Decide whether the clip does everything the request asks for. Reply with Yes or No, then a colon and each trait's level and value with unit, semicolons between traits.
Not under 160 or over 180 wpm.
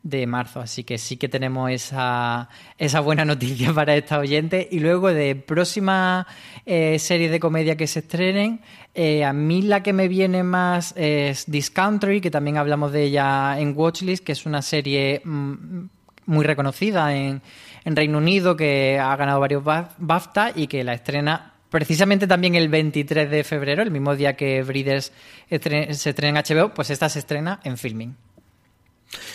Yes: average, 170 wpm